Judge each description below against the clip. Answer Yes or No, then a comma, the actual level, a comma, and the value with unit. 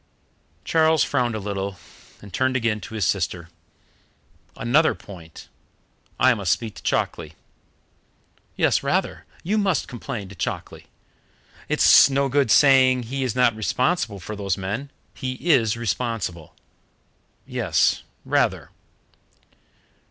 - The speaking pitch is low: Yes, low, 115 Hz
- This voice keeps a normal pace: No, slow, 120 wpm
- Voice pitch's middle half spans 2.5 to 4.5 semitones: No, average, 5.0 semitones